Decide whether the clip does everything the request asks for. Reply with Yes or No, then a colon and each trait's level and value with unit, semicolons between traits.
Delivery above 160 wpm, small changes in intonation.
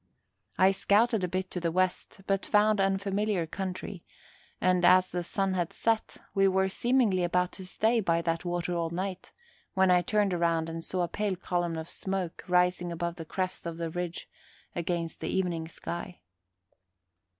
Yes: average, 170 wpm; narrow, 2.1 semitones